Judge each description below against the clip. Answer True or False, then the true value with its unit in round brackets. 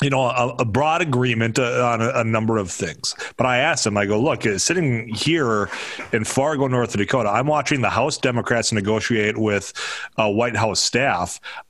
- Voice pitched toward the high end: False (120 Hz)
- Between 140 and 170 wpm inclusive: False (195 wpm)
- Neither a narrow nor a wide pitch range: True (3.2 semitones)